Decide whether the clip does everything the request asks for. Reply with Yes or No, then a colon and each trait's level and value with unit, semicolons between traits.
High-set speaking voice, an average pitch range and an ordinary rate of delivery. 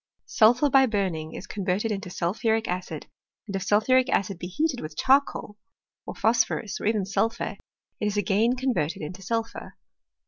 Yes: high, 210 Hz; average, 3.8 semitones; average, 165 wpm